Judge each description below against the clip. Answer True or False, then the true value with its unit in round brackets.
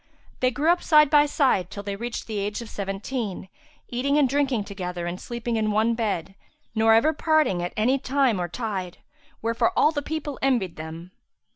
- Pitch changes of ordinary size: False (5.8 semitones)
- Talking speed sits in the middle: True (185 wpm)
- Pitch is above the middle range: True (230 Hz)